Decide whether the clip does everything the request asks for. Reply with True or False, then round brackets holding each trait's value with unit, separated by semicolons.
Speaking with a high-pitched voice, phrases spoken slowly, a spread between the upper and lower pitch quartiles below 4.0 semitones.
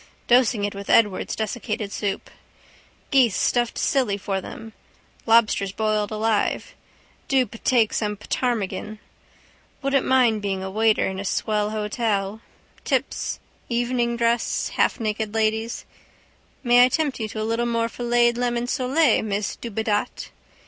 True (225 Hz; 130 wpm; 2.4 semitones)